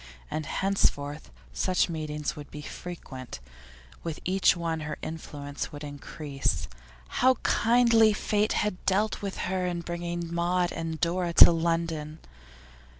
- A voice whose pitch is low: No, medium, 170 Hz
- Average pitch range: Yes, average, 3.4 semitones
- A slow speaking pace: Yes, slow, 130 wpm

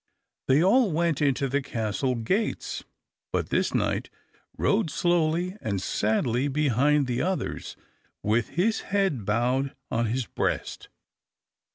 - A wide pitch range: Yes, wide, 6.4 semitones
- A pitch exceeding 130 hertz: Yes, medium, 140 Hz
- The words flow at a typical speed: No, slow, 125 wpm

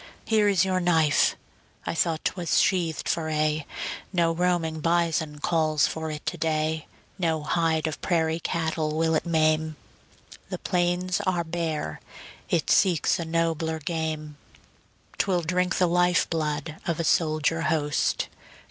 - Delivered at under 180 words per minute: Yes, average, 140 wpm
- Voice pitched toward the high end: No, medium, 160 Hz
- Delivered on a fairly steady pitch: Yes, narrow, 1.8 semitones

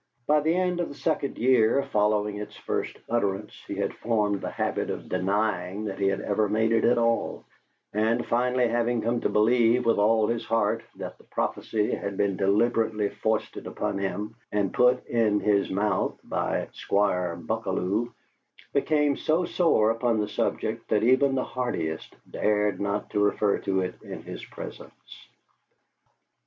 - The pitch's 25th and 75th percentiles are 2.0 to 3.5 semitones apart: Yes, average, 2.8 semitones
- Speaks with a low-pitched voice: Yes, low, 110 Hz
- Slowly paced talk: No, average, 160 wpm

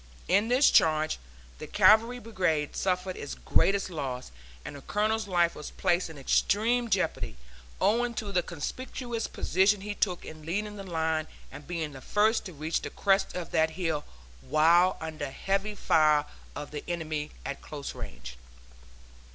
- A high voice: No, medium, 175 Hz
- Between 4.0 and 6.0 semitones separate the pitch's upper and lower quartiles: Yes, average, 5.1 semitones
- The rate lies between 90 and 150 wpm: No, average, 160 wpm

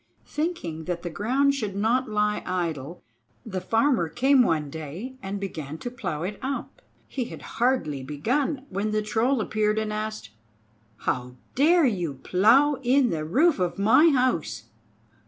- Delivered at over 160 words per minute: No, average, 155 wpm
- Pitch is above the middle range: Yes, high, 210 Hz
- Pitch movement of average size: No, wide, 7.2 semitones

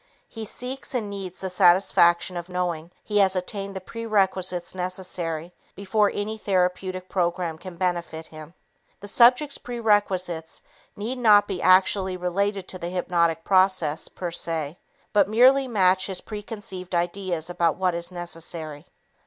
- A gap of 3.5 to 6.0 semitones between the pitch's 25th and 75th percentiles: No, average, 2.8 semitones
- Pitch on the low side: No, medium, 185 Hz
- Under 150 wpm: Yes, average, 140 wpm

